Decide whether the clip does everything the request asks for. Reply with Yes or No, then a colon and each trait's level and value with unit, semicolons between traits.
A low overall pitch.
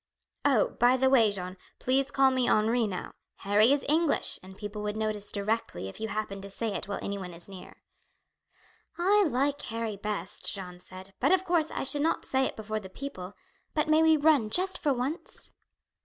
No: high, 225 Hz